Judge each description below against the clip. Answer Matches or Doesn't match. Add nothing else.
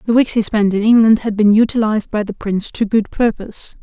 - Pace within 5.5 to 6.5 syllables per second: Matches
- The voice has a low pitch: Doesn't match